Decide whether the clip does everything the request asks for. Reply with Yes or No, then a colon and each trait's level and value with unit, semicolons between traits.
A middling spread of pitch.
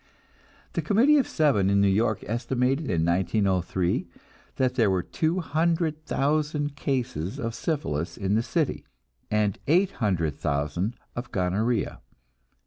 No: wide, 8.0 semitones